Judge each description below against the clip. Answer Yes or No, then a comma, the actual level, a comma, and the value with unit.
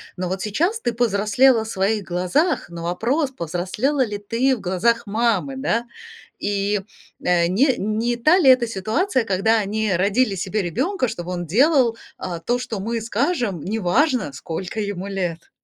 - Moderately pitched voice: No, high, 215 Hz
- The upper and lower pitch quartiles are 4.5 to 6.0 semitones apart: Yes, average, 4.9 semitones